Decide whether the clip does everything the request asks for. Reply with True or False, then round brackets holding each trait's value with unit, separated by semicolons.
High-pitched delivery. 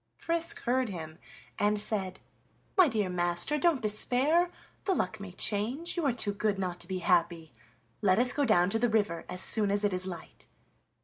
True (205 Hz)